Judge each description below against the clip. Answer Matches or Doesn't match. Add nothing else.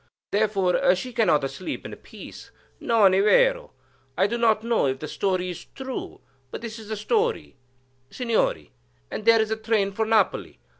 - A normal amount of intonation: Matches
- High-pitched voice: Matches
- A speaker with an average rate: Matches